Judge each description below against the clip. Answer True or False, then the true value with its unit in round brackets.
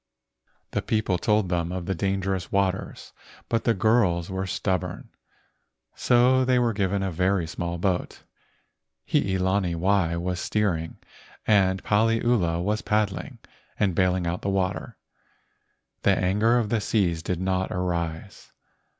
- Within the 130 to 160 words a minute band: True (140 wpm)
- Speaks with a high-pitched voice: False (95 Hz)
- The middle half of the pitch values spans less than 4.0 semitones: True (2.9 semitones)